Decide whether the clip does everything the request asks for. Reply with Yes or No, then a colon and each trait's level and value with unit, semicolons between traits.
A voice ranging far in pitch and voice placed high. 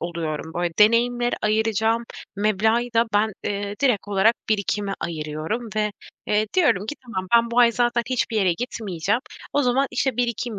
No: average, 3.3 semitones; high, 220 Hz